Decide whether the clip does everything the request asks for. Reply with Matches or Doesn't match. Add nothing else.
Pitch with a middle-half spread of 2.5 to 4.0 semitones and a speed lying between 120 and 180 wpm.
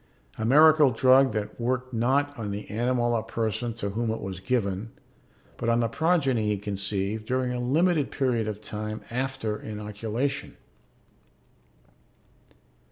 Matches